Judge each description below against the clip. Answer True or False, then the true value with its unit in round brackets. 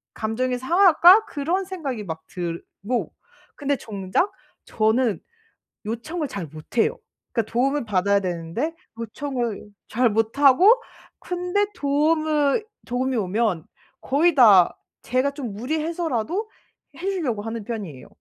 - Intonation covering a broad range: True (6.4 semitones)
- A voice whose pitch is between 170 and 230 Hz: False (255 Hz)